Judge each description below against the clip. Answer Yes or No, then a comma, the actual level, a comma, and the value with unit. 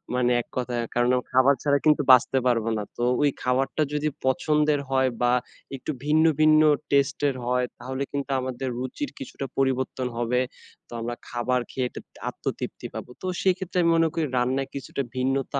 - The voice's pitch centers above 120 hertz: Yes, low, 130 Hz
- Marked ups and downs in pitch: No, average, 2.8 semitones